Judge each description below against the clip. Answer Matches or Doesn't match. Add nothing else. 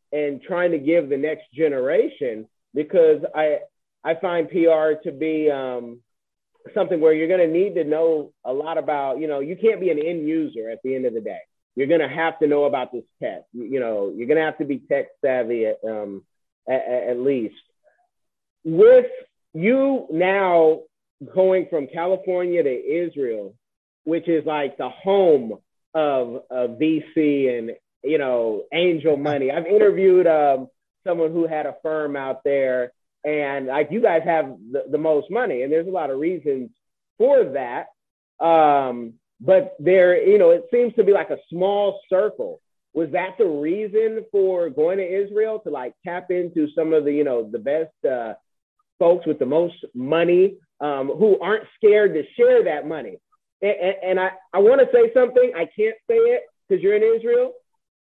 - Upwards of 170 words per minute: Matches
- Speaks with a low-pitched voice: Doesn't match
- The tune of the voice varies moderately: Doesn't match